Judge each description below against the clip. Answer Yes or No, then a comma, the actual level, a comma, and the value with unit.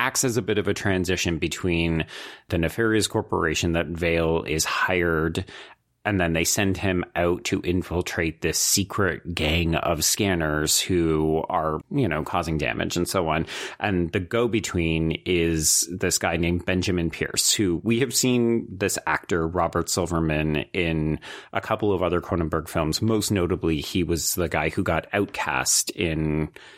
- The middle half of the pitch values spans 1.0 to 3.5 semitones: Yes, average, 2.9 semitones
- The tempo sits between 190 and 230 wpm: No, average, 160 wpm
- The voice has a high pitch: No, very low, 85 Hz